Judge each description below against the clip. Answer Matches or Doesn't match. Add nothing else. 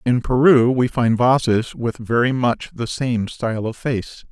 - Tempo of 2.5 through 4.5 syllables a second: Matches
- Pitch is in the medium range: Doesn't match